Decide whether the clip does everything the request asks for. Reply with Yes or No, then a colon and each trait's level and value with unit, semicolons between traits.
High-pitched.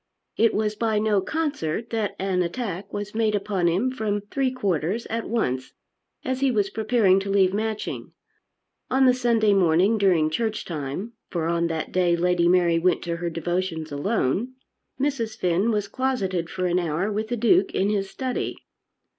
Yes: high, 200 Hz